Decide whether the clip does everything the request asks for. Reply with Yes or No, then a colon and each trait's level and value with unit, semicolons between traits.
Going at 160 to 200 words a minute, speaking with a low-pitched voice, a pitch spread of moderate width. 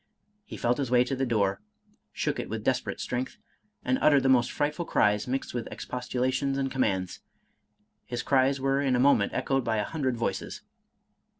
No: average, 180 wpm; low, 130 Hz; narrow, 2.3 semitones